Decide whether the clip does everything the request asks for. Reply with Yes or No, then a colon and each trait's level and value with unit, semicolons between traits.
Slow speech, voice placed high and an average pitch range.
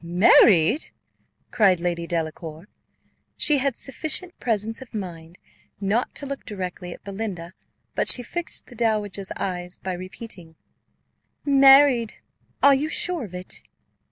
No: slow, 130 wpm; high, 205 Hz; wide, 6.8 semitones